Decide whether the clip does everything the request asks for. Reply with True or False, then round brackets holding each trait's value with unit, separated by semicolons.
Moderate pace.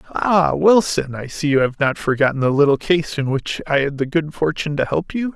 False (235 wpm)